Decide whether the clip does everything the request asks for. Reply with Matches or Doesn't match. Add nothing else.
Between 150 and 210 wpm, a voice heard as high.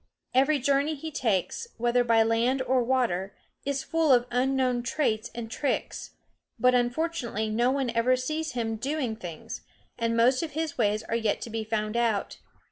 Matches